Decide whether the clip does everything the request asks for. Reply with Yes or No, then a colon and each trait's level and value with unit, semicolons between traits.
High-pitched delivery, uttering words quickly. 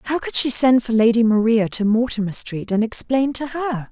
Yes: high, 240 Hz; fast, 215 wpm